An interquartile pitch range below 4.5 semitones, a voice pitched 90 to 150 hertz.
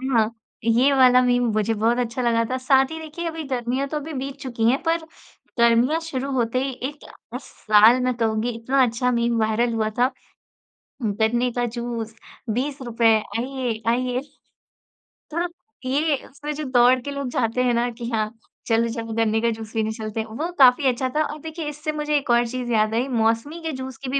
No: average, 3.0 semitones; high, 245 Hz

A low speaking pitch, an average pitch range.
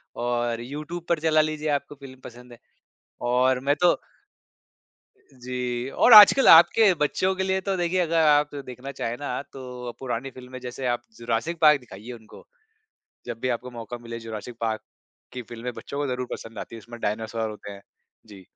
Yes: low, 125 Hz; average, 4.2 semitones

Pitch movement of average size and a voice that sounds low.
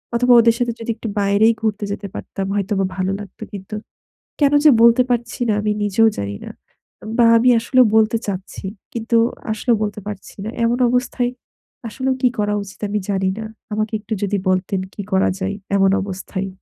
No: average, 3.0 semitones; high, 210 Hz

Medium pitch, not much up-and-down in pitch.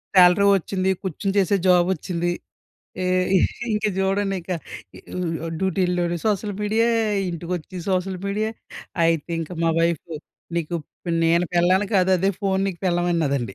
Yes: medium, 180 Hz; narrow, 2.2 semitones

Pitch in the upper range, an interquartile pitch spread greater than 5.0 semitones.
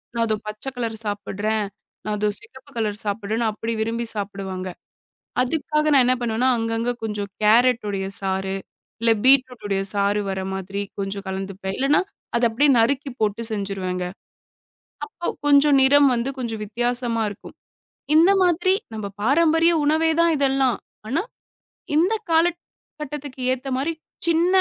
Yes: high, 230 Hz; wide, 5.6 semitones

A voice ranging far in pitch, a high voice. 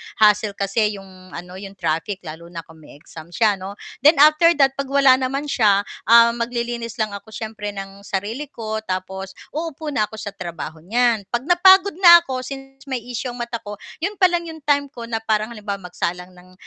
Yes: wide, 5.7 semitones; high, 220 Hz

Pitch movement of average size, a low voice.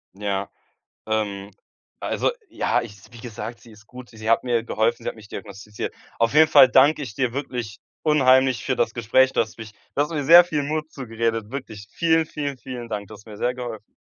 Yes: average, 3.7 semitones; low, 120 Hz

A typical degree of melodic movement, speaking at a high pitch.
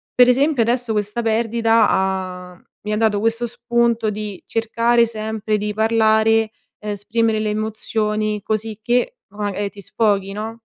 No: narrow, 1.6 semitones; high, 220 Hz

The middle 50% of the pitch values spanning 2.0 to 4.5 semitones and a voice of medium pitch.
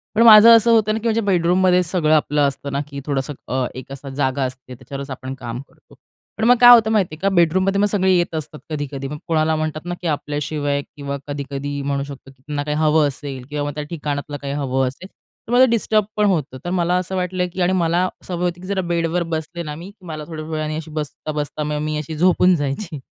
Yes: average, 4.1 semitones; medium, 155 Hz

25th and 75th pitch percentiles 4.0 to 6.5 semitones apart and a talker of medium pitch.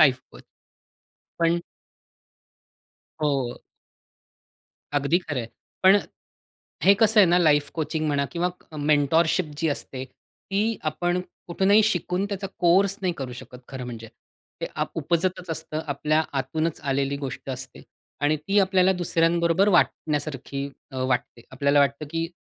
Yes: average, 4.3 semitones; medium, 155 Hz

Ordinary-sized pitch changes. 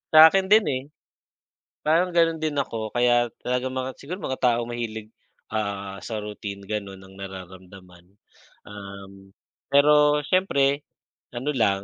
No: wide, 6.7 semitones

